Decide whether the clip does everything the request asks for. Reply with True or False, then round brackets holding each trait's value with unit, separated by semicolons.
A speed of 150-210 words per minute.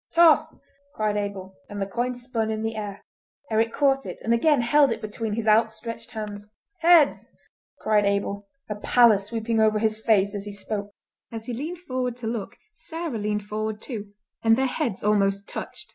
True (180 wpm)